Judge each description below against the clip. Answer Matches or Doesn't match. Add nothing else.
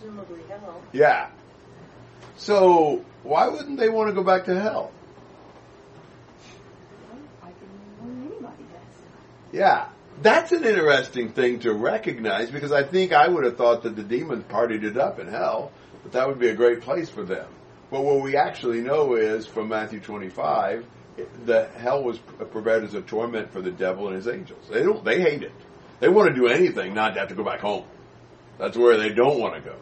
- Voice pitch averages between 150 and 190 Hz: Doesn't match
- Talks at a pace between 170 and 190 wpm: Matches